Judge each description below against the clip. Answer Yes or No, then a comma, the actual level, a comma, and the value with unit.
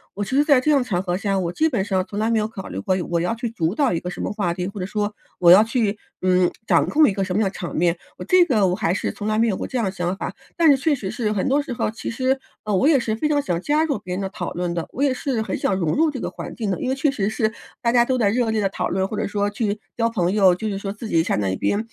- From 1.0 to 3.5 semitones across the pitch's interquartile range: No, average, 4.8 semitones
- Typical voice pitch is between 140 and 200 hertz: No, high, 210 Hz